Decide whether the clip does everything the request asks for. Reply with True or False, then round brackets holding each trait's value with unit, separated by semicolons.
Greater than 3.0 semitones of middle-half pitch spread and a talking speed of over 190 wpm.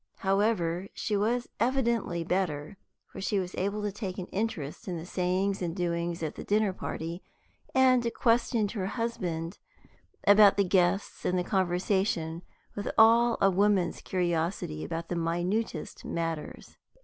False (3.4 semitones; 145 wpm)